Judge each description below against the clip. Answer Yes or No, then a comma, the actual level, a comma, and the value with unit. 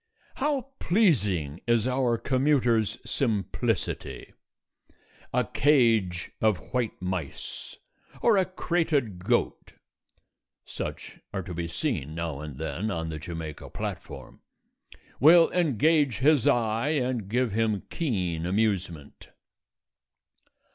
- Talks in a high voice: No, low, 110 Hz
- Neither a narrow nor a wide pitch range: No, wide, 7.8 semitones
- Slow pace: Yes, slow, 105 wpm